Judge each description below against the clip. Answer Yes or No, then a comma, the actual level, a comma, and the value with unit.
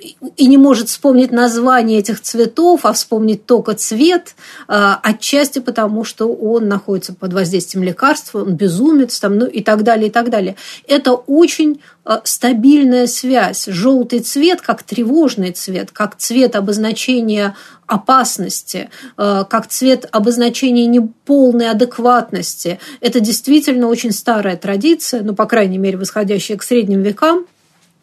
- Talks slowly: No, average, 130 wpm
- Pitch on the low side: No, high, 230 Hz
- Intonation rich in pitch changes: No, average, 3.8 semitones